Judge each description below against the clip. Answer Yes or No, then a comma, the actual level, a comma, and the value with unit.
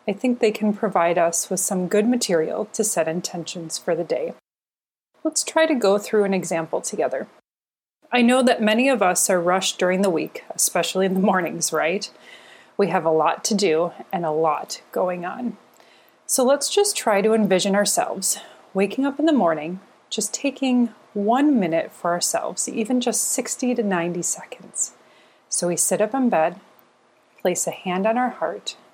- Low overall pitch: No, high, 200 Hz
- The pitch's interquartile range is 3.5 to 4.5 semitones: No, average, 5.3 semitones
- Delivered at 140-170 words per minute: No, average, 180 wpm